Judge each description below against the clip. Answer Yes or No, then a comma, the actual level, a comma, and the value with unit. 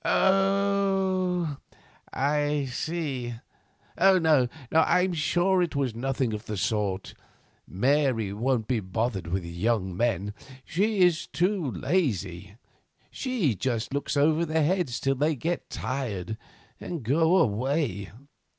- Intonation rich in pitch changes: Yes, wide, 7.5 semitones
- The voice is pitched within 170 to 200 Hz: No, medium, 140 Hz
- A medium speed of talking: No, slow, 120 wpm